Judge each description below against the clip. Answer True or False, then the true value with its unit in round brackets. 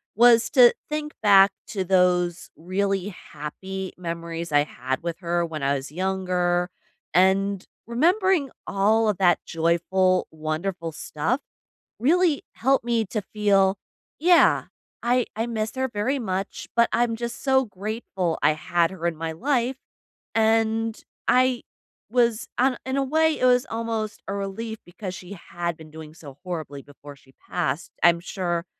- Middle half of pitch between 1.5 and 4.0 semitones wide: False (5.5 semitones)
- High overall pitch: True (195 Hz)